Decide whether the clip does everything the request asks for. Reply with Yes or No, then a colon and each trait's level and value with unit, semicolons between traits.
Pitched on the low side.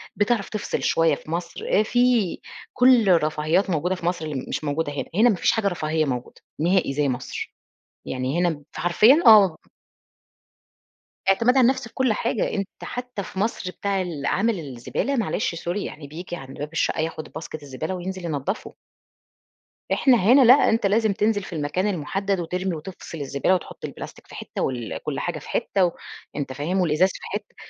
No: medium, 180 Hz